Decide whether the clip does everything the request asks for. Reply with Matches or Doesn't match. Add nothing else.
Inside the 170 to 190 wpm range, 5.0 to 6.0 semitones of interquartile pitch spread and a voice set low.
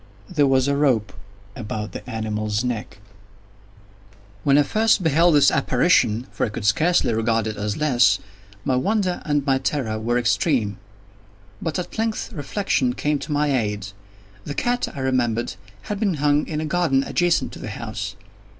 Doesn't match